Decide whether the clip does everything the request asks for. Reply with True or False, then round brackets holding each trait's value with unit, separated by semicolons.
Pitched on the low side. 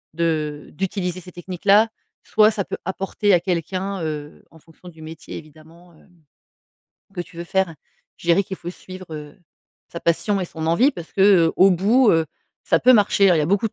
False (175 Hz)